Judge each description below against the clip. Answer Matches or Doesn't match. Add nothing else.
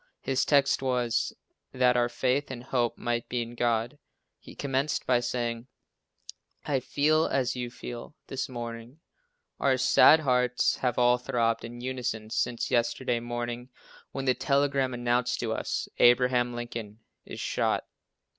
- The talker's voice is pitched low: Matches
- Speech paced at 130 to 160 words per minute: Matches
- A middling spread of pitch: Doesn't match